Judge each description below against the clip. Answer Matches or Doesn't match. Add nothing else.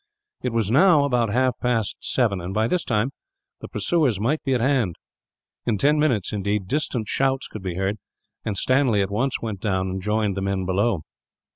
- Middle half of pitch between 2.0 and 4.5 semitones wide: Doesn't match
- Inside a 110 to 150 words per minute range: Doesn't match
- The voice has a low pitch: Matches